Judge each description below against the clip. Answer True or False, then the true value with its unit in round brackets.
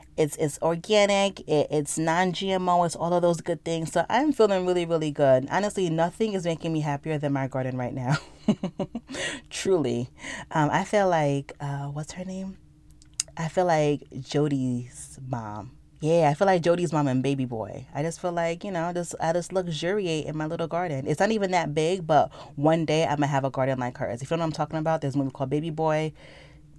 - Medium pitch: True (160 Hz)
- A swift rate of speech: True (215 wpm)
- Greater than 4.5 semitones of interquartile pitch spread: False (3.6 semitones)